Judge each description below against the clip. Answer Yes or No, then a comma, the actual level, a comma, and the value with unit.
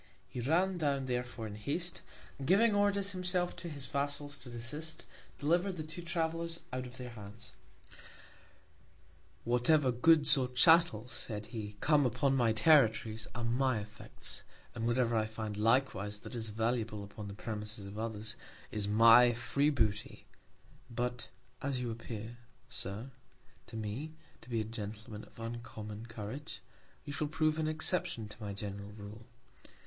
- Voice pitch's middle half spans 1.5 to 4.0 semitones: No, average, 5.3 semitones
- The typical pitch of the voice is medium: No, low, 120 Hz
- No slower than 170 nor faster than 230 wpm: No, average, 155 wpm